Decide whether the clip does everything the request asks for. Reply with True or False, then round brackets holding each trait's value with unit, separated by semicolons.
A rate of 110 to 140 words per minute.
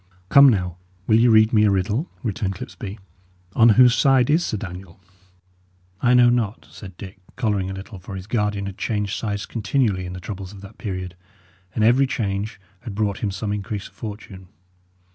False (185 wpm)